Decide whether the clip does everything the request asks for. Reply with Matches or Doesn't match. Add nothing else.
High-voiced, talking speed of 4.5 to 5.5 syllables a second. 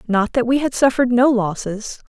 Matches